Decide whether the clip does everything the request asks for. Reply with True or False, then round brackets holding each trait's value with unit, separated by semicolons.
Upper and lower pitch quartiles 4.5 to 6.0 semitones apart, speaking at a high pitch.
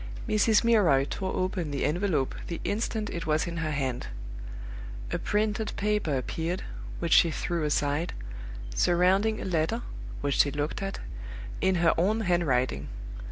False (5.2 semitones; 175 Hz)